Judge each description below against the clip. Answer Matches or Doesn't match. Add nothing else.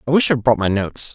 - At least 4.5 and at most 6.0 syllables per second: Doesn't match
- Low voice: Matches